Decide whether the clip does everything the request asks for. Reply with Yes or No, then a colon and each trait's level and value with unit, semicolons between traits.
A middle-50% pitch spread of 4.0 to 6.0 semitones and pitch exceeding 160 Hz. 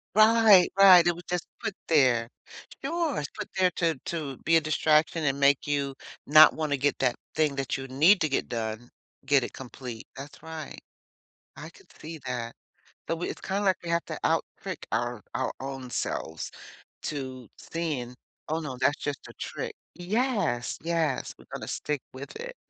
No: average, 4.4 semitones; medium, 150 Hz